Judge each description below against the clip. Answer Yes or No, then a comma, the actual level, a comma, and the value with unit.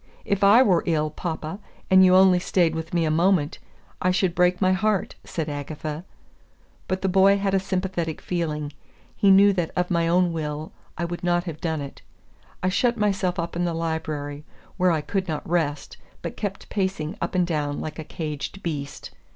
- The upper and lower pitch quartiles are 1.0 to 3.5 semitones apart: Yes, average, 3.1 semitones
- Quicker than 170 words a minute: Yes, average, 190 wpm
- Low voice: No, medium, 175 Hz